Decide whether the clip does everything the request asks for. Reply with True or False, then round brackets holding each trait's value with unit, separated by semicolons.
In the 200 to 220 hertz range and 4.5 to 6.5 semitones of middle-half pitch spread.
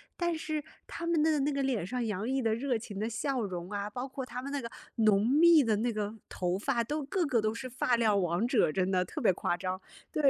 False (235 Hz; 5.3 semitones)